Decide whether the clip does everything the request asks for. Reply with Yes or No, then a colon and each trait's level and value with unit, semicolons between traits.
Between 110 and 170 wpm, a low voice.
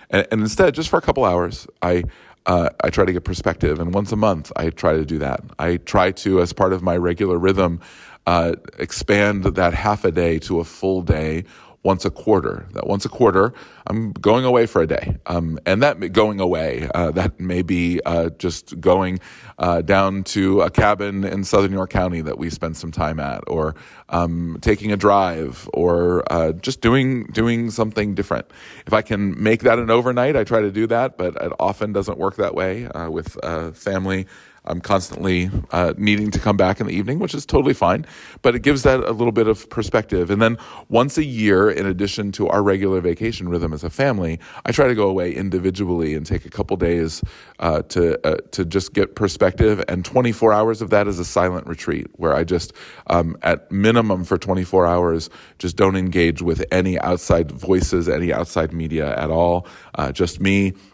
No: fast, 205 wpm; very low, 95 Hz